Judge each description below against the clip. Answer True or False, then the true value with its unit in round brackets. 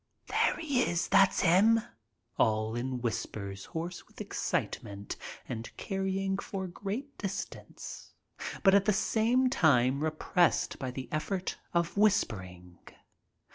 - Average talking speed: False (120 wpm)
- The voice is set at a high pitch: False (175 Hz)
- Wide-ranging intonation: True (8.6 semitones)